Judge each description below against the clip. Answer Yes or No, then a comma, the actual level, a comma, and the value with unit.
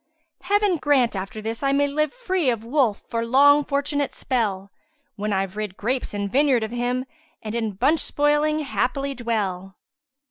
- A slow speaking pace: No, average, 175 wpm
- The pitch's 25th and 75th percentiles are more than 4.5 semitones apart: Yes, average, 5.2 semitones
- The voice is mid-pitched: No, very high, 250 Hz